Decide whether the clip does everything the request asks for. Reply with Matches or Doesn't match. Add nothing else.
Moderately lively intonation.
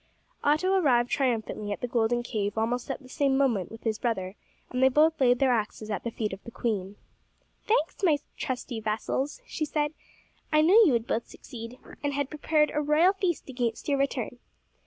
Matches